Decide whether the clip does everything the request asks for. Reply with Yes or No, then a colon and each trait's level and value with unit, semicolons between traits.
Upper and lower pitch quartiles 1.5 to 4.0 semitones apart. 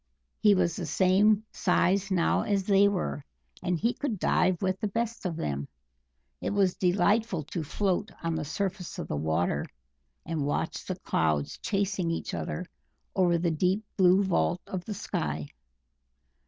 Yes: average, 3.3 semitones